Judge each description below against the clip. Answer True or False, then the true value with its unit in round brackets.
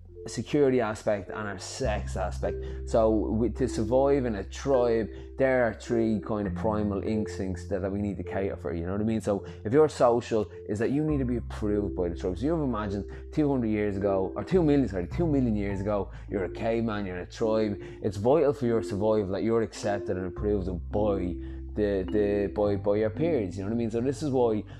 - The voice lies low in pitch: True (105 Hz)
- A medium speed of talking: False (230 wpm)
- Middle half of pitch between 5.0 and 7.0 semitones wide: False (3.4 semitones)